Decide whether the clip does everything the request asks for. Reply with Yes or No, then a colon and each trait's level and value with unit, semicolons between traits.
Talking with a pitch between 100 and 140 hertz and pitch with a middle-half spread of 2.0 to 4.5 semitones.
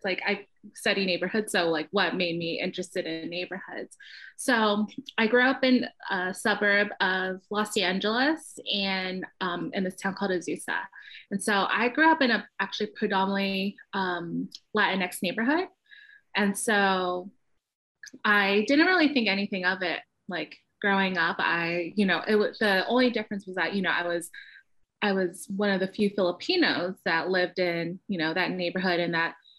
No: high, 195 Hz; average, 2.8 semitones